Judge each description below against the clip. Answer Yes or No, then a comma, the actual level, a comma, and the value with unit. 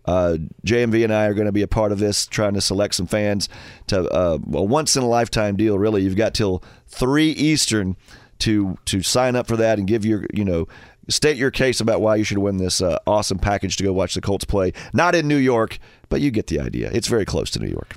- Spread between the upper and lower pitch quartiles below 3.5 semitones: Yes, average, 3.1 semitones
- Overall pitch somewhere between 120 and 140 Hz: No, low, 105 Hz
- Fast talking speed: Yes, fast, 240 wpm